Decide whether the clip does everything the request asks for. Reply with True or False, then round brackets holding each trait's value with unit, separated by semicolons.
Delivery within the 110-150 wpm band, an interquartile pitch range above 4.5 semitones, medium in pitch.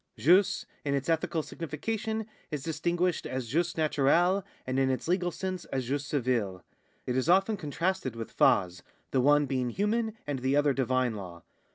False (170 wpm; 5.4 semitones; 145 Hz)